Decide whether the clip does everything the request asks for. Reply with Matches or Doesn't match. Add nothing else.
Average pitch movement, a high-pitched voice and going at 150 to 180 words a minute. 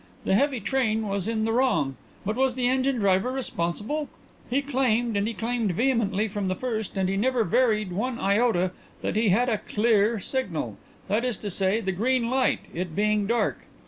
Doesn't match